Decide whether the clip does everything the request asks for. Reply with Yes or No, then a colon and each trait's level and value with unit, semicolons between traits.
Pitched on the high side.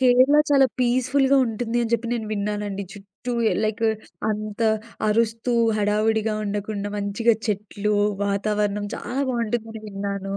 Yes: high, 215 Hz